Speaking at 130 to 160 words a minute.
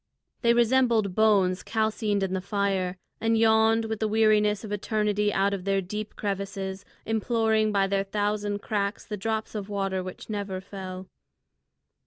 Yes: average, 155 wpm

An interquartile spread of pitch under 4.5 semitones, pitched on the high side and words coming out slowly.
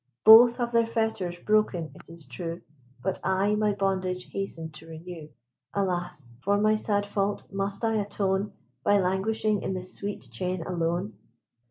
No: average, 3.0 semitones; high, 195 Hz; average, 155 wpm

